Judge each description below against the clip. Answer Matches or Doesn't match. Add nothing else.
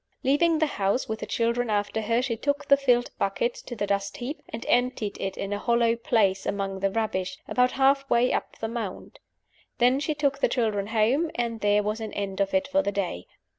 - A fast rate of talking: Matches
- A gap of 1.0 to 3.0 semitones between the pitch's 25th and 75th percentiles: Doesn't match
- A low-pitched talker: Doesn't match